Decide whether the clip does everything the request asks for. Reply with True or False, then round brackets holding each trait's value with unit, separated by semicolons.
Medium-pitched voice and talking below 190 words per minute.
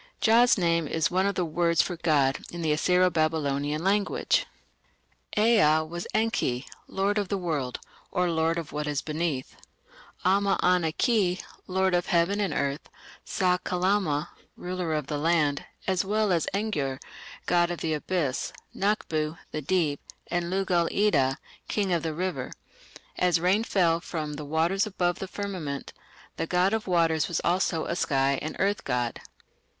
True (170 Hz; 160 wpm)